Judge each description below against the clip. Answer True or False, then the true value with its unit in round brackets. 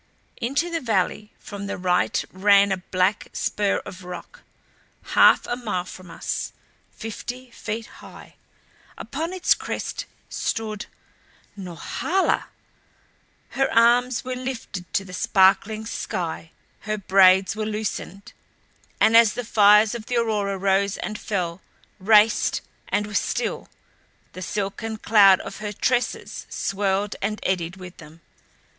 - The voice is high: True (205 Hz)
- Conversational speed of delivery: False (130 wpm)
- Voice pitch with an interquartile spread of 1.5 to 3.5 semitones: True (3.0 semitones)